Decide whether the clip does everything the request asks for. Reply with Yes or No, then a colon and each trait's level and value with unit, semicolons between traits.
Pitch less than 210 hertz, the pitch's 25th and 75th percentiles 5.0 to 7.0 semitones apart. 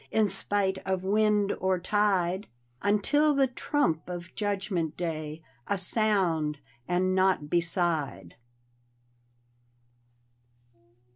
No: medium, 185 Hz; average, 3.4 semitones